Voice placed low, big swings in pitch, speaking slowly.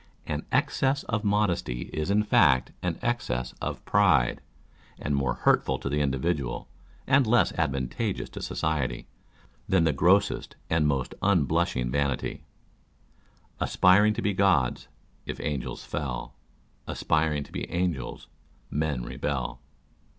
Yes: very low, 75 Hz; wide, 6.7 semitones; slow, 130 wpm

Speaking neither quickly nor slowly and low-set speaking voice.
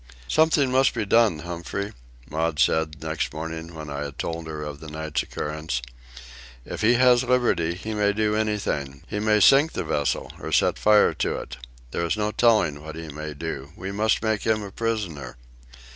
Yes: average, 190 wpm; very low, 85 Hz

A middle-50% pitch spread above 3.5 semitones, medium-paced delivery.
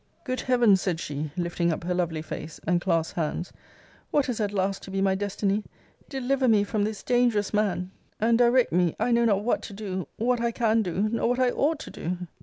No: average, 4.6 semitones; fast, 215 wpm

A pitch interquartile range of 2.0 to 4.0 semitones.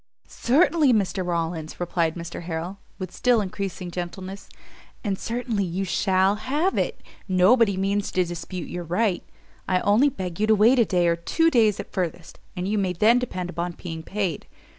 Yes: average, 3.5 semitones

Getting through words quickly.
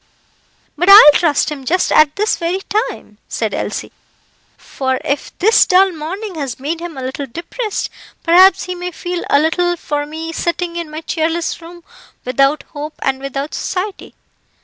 No: average, 170 wpm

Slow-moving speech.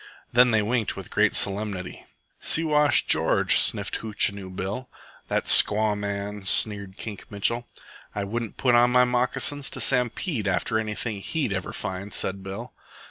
No: average, 145 wpm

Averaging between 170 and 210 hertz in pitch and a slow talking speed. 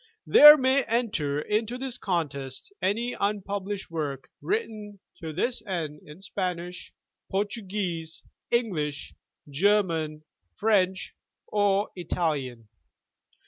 Yes: high, 190 Hz; slow, 95 wpm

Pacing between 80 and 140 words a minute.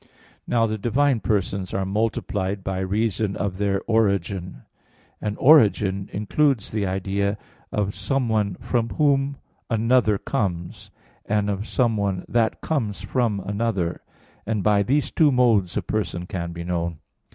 Yes: slow, 135 wpm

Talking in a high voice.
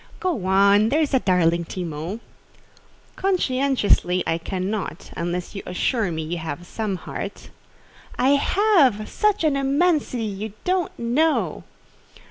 Yes: high, 215 Hz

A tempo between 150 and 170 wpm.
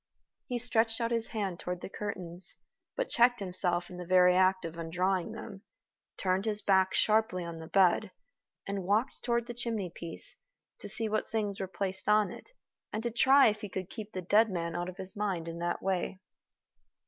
No: average, 195 wpm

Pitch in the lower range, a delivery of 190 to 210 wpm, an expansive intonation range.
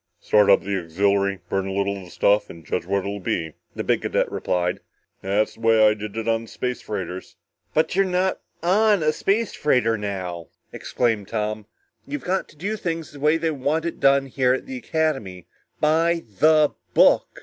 Yes: low, 115 Hz; average, 195 wpm; wide, 8.1 semitones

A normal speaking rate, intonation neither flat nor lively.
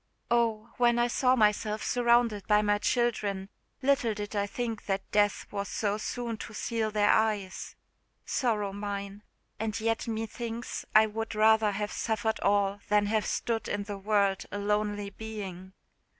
No: average, 160 wpm; narrow, 1.8 semitones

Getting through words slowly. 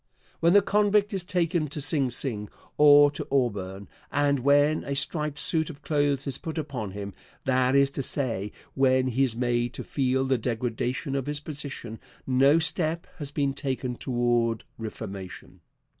No: average, 165 wpm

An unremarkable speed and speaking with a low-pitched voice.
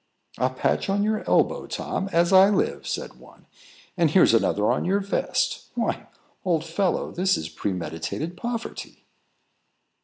No: average, 145 wpm; medium, 175 Hz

